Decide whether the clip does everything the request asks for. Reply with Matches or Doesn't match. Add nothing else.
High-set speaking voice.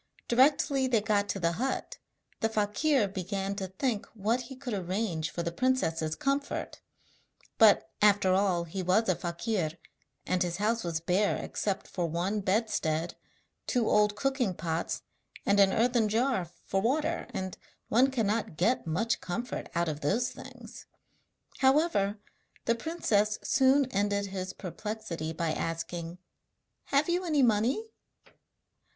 Matches